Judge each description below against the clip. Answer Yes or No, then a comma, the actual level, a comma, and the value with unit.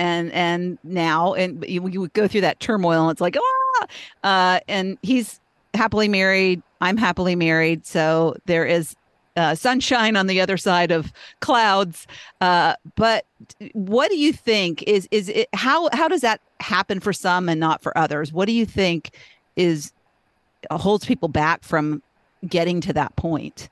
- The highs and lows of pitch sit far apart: No, average, 4.0 semitones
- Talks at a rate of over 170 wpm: No, average, 165 wpm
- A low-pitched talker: No, medium, 180 Hz